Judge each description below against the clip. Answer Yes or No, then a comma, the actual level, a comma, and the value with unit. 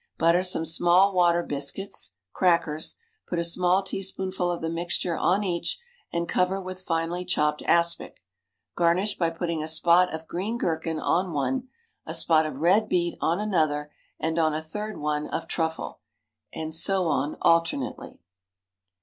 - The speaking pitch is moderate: Yes, medium, 170 Hz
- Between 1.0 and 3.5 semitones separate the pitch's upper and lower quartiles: Yes, narrow, 2.4 semitones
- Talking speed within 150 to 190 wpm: Yes, average, 155 wpm